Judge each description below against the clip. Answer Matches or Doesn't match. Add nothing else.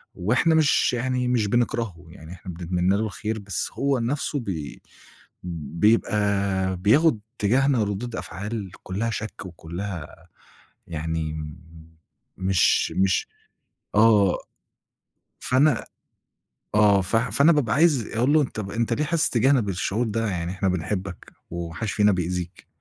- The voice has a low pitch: Matches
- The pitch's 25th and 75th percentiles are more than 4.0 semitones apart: Matches